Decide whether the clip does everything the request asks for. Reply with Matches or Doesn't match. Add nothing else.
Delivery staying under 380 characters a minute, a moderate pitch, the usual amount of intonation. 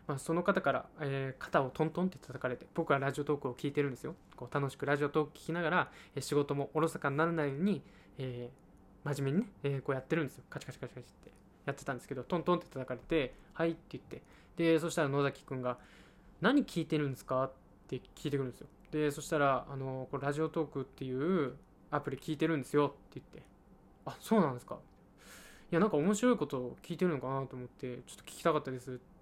Doesn't match